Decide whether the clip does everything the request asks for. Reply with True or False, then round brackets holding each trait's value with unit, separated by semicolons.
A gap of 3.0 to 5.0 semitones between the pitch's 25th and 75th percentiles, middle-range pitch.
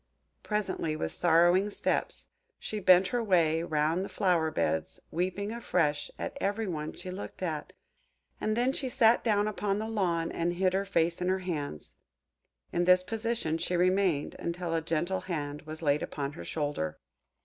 True (4.0 semitones; 180 Hz)